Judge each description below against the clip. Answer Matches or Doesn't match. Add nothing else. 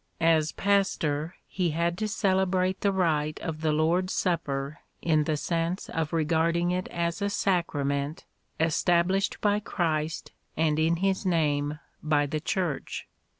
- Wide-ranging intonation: Doesn't match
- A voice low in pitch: Doesn't match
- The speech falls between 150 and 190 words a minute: Doesn't match